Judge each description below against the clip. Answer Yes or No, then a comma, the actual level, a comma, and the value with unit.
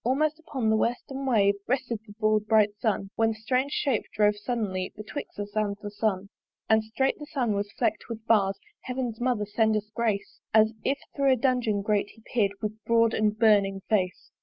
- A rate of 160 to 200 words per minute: Yes, average, 195 wpm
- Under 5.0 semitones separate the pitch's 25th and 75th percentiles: Yes, average, 2.9 semitones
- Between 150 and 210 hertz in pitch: No, high, 220 Hz